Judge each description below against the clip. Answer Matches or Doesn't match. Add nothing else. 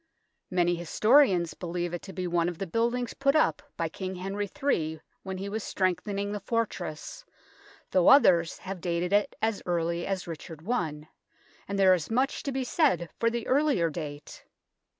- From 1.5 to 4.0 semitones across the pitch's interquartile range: Doesn't match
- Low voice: Doesn't match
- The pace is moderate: Matches